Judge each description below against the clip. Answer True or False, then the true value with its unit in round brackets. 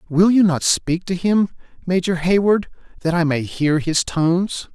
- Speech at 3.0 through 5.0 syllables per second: True (4.3 syllables/s)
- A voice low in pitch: False (175 Hz)